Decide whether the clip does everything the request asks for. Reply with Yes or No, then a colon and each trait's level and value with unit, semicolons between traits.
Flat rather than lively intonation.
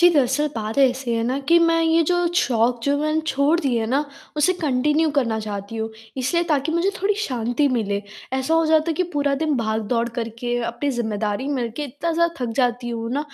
No: average, 4.9 semitones